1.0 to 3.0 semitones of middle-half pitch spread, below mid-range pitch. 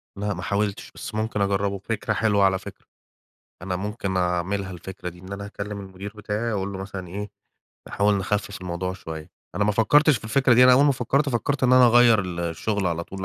Yes: average, 2.7 semitones; low, 100 Hz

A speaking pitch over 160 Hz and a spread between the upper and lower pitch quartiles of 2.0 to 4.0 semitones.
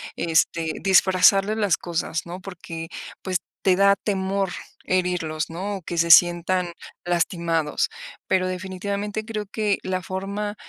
Yes: medium, 185 Hz; narrow, 2.6 semitones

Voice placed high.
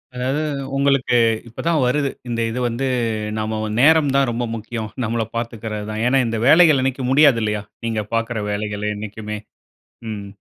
No: low, 115 Hz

